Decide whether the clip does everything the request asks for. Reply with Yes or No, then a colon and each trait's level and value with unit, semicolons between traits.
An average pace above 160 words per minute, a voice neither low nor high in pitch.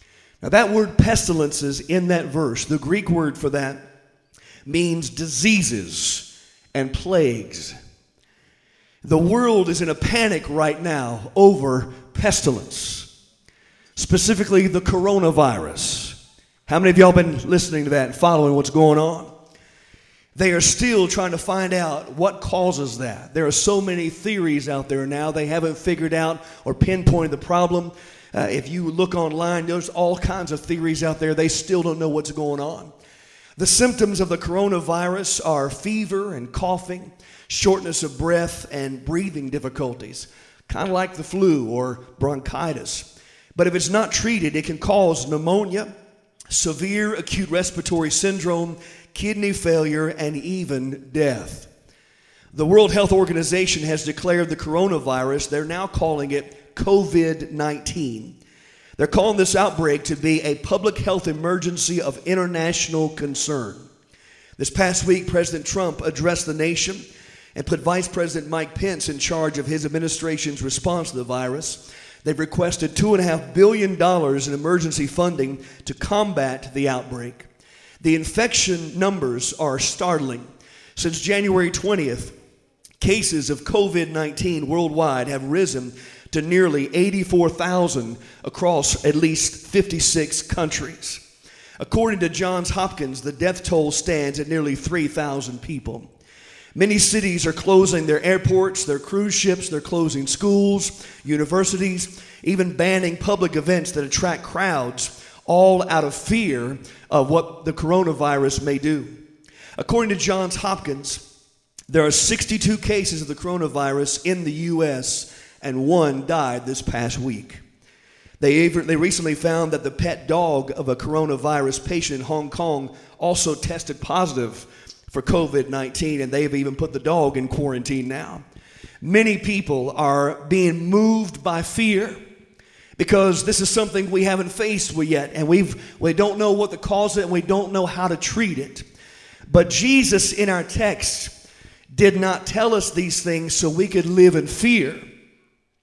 No: average, 145 wpm; medium, 165 Hz